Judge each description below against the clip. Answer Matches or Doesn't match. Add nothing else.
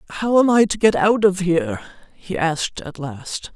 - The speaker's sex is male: Matches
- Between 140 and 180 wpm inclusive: Doesn't match